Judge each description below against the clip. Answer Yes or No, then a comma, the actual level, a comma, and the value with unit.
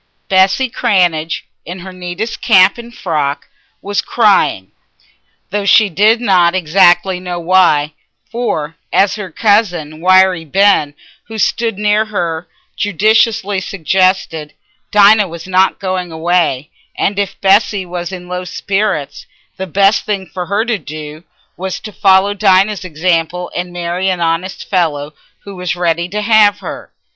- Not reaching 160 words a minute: Yes, average, 140 wpm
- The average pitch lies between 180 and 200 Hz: Yes, medium, 185 Hz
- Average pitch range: Yes, average, 3.0 semitones